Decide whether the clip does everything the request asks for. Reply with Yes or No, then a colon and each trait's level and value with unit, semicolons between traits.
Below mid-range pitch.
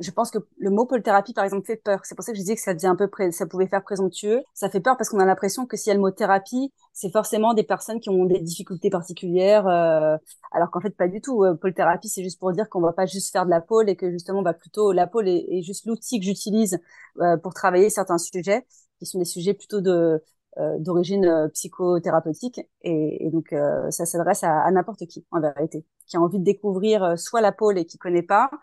No: high, 190 Hz